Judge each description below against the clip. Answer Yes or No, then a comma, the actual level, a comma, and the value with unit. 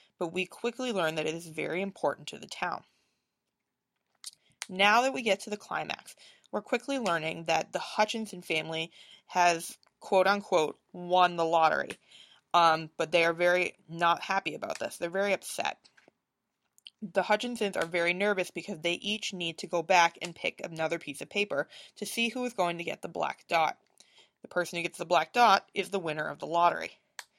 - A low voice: No, medium, 180 Hz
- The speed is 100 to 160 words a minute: No, average, 185 wpm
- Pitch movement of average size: Yes, average, 3.5 semitones